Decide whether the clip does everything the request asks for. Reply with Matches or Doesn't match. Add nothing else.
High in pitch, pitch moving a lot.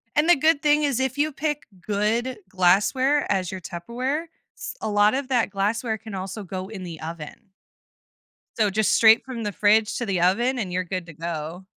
Matches